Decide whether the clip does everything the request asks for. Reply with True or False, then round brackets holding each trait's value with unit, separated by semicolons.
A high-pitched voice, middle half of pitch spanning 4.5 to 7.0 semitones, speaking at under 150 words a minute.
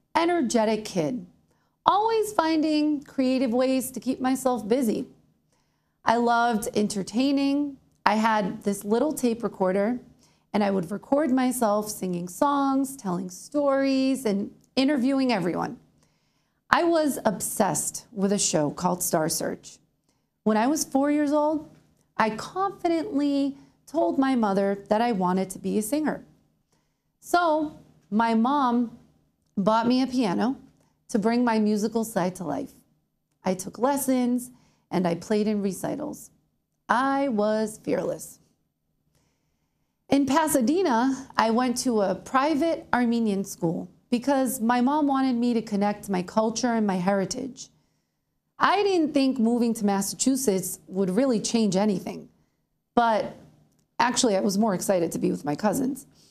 True (235 Hz; 4.9 semitones; 135 wpm)